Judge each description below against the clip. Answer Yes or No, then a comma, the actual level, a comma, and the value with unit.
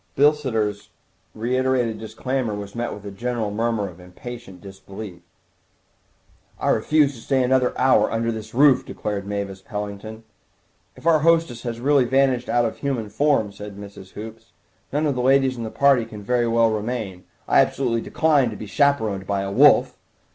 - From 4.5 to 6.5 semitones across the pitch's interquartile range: No, average, 4.1 semitones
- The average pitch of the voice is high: No, low, 115 Hz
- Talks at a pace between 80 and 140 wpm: No, average, 170 wpm